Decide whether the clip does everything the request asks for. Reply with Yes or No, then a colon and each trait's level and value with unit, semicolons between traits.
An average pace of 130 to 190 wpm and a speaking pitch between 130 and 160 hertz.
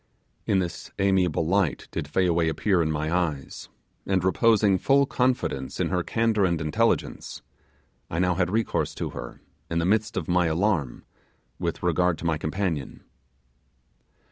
No: average, 150 wpm; very low, 90 Hz